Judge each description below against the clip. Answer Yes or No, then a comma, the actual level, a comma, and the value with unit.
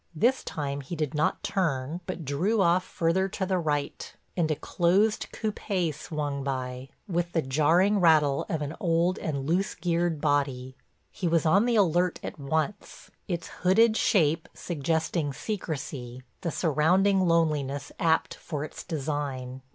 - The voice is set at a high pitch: No, medium, 160 Hz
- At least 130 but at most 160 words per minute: Yes, average, 150 wpm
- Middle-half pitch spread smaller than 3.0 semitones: No, average, 4.1 semitones